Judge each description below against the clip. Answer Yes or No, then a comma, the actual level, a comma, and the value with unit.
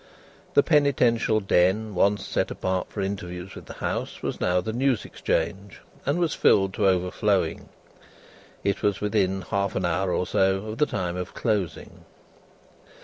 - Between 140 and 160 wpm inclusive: Yes, average, 155 wpm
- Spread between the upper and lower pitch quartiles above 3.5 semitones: No, average, 3.0 semitones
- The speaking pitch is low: Yes, low, 100 Hz